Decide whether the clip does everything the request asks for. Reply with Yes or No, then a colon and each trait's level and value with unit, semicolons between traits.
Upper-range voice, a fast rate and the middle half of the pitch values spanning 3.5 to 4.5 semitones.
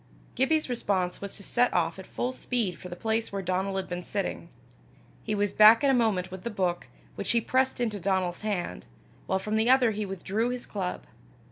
Yes: high, 205 Hz; fast, 210 wpm; average, 4.0 semitones